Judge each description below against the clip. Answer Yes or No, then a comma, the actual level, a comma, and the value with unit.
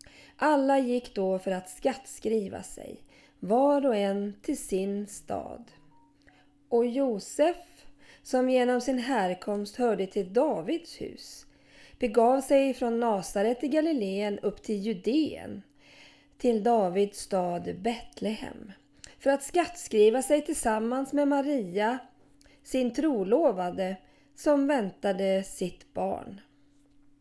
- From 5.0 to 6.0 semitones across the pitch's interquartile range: Yes, wide, 5.5 semitones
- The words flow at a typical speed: No, slow, 110 wpm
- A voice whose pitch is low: No, high, 235 Hz